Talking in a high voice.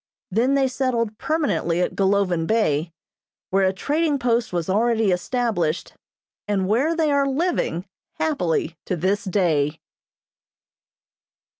Yes: high, 210 Hz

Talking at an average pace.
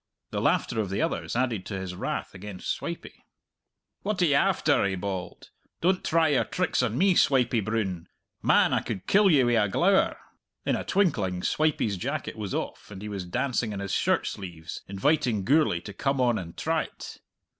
Yes: average, 190 wpm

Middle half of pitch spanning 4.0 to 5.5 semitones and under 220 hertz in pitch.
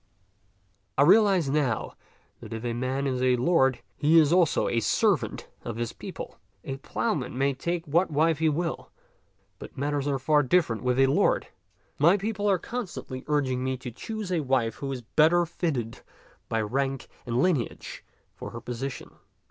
Yes: average, 4.6 semitones; medium, 140 Hz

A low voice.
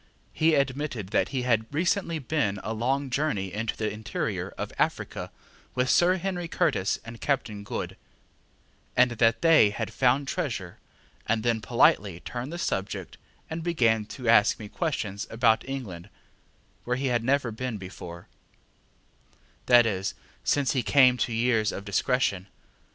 Yes: low, 120 Hz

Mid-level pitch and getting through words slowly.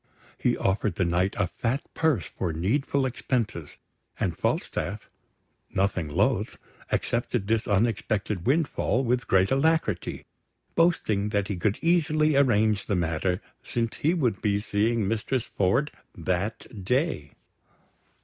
No: low, 110 Hz; slow, 125 wpm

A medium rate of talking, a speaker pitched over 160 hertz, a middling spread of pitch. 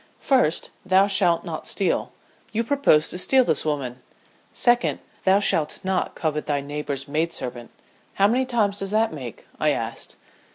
No: average, 160 wpm; medium, 185 Hz; wide, 6.5 semitones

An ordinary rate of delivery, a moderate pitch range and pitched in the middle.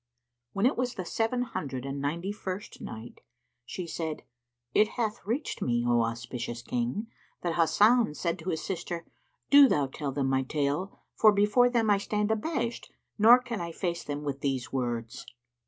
No: average, 170 wpm; wide, 8.0 semitones; medium, 170 Hz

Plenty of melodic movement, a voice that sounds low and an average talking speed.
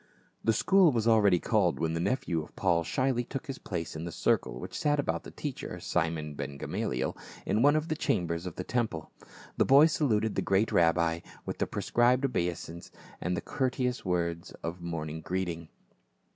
Yes: wide, 7.1 semitones; very low, 90 Hz; average, 185 wpm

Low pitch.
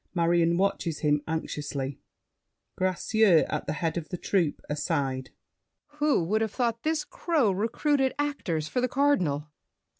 No: medium, 180 Hz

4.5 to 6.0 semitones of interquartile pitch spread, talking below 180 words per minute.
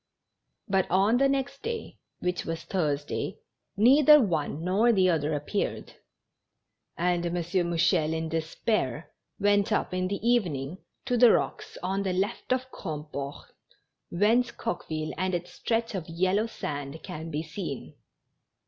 Yes: average, 5.1 semitones; average, 140 wpm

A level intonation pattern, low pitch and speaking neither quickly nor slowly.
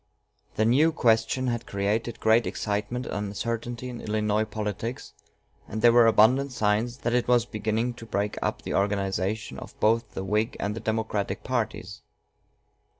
Yes: narrow, 2.3 semitones; low, 110 Hz; average, 155 wpm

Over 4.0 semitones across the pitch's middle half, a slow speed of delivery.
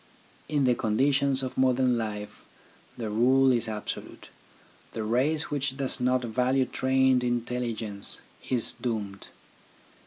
No: average, 2.7 semitones; slow, 120 wpm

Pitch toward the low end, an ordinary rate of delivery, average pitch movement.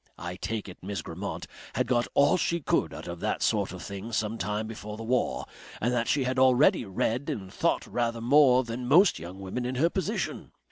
No: low, 115 Hz; fast, 215 wpm; average, 4.2 semitones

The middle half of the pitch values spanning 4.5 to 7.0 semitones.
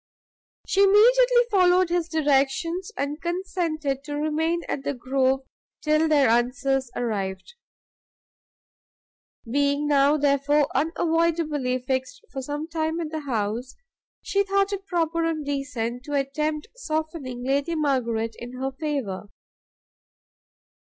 No: average, 3.8 semitones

